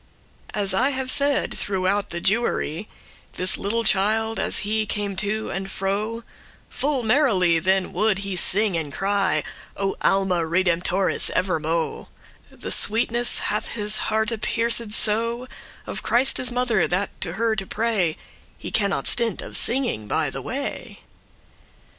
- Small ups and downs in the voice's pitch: No, average, 3.3 semitones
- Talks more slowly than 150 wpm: Yes, average, 140 wpm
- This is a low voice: No, high, 205 Hz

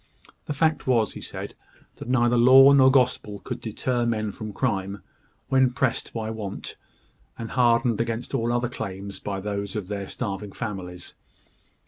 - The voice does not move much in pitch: No, average, 3.7 semitones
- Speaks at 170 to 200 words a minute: No, average, 155 wpm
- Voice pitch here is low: Yes, low, 115 Hz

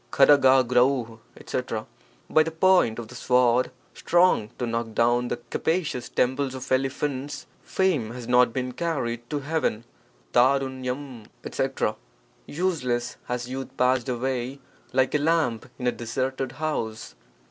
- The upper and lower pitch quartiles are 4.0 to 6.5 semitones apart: No, average, 2.8 semitones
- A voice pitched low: Yes, low, 130 Hz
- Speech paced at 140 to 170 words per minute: Yes, average, 150 wpm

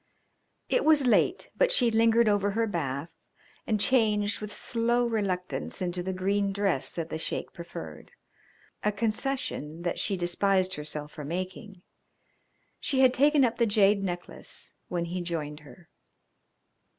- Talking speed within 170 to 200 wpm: No, average, 145 wpm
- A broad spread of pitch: No, average, 4.7 semitones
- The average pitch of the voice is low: No, high, 200 Hz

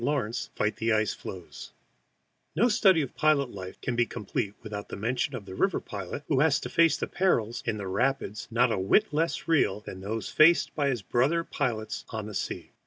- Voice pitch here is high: No, low, 120 Hz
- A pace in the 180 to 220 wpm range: Yes, average, 195 wpm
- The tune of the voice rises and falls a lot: Yes, wide, 6.0 semitones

